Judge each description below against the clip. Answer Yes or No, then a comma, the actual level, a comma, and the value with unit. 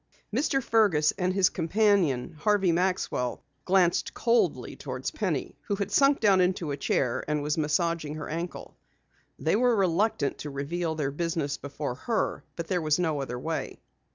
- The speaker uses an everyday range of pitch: Yes, average, 4.7 semitones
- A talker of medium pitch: Yes, medium, 170 Hz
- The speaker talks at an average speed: Yes, average, 160 wpm